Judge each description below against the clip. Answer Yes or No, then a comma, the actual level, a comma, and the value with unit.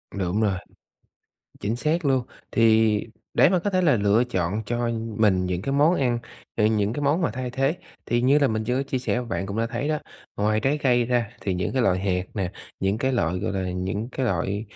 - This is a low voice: Yes, low, 115 Hz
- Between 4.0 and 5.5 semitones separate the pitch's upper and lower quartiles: Yes, average, 5.0 semitones